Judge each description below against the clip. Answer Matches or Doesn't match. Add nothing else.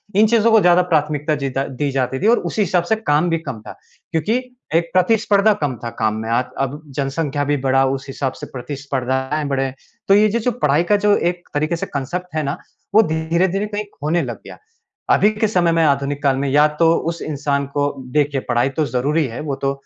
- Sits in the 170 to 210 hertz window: Doesn't match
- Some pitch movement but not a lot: Matches